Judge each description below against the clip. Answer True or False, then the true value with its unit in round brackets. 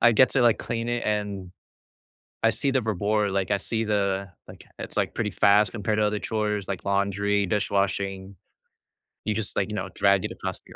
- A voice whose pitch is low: True (105 Hz)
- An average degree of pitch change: False (1.6 semitones)